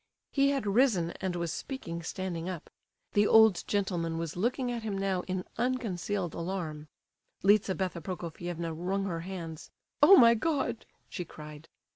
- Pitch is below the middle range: No, medium, 185 Hz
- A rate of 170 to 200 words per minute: No, average, 145 wpm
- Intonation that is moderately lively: Yes, average, 4.4 semitones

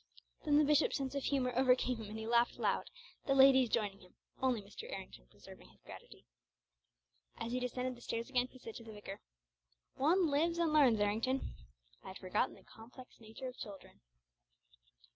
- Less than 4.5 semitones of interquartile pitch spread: Yes, average, 3.5 semitones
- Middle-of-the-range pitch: No, very high, 250 Hz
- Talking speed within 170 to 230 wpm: Yes, average, 180 wpm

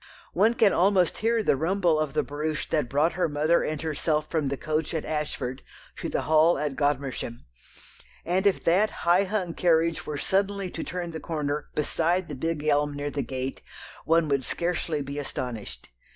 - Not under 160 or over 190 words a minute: Yes, average, 180 wpm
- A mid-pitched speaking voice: Yes, medium, 155 Hz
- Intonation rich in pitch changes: No, average, 3.3 semitones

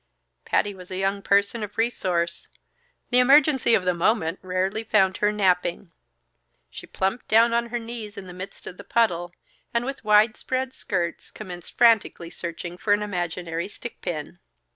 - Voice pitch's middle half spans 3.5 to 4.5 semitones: Yes, average, 4.2 semitones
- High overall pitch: Yes, high, 200 Hz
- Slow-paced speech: No, average, 165 wpm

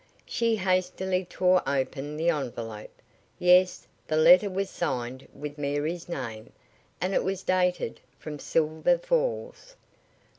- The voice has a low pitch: No, medium, 175 Hz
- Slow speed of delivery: Yes, slow, 120 wpm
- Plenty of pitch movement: No, average, 4.4 semitones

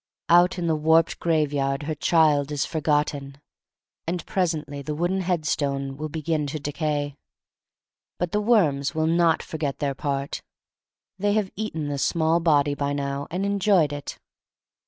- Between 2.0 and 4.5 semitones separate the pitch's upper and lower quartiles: Yes, average, 2.9 semitones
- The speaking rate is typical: Yes, average, 150 wpm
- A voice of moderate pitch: Yes, medium, 155 Hz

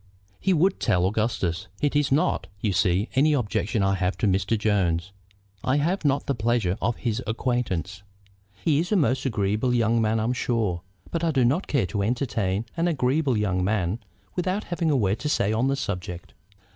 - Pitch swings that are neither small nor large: No, wide, 6.0 semitones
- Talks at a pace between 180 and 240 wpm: Yes, average, 190 wpm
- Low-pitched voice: Yes, low, 115 Hz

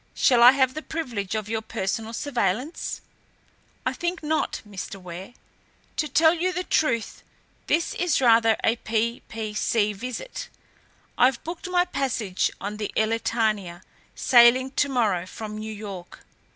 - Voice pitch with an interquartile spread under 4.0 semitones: No, average, 4.7 semitones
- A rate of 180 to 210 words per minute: No, average, 140 wpm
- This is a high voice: Yes, high, 230 Hz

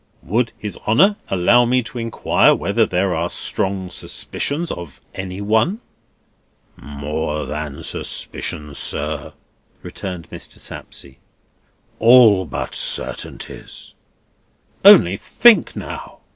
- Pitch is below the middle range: Yes, very low, 95 Hz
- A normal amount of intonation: No, wide, 6.6 semitones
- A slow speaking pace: Yes, slow, 105 wpm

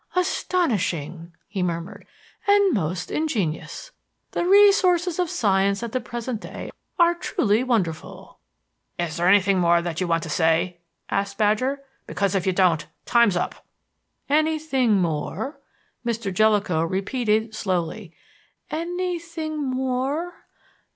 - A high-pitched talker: Yes, high, 215 Hz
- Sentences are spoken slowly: Yes, slow, 120 wpm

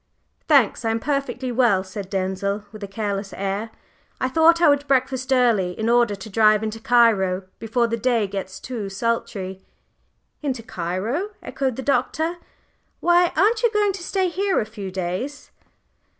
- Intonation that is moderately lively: No, wide, 5.8 semitones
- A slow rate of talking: No, average, 165 wpm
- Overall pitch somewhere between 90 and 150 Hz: No, high, 230 Hz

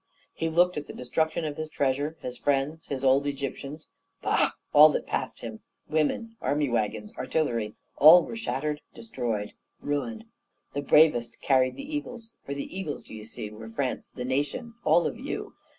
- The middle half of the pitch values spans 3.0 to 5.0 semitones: Yes, average, 3.8 semitones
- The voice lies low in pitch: No, medium, 145 Hz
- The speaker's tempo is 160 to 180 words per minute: Yes, average, 165 wpm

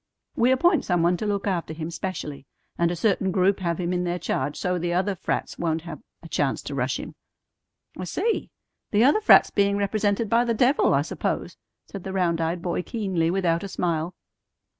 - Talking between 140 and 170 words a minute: No, fast, 205 wpm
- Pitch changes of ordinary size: Yes, average, 3.2 semitones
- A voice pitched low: No, medium, 180 Hz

